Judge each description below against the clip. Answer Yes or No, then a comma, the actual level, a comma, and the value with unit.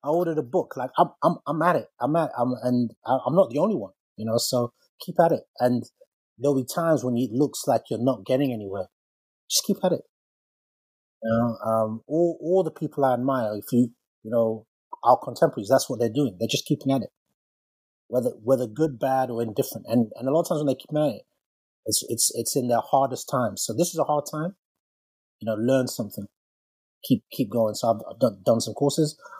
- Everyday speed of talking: No, fast, 220 wpm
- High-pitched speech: No, low, 125 Hz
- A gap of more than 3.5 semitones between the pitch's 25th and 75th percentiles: Yes, average, 4.4 semitones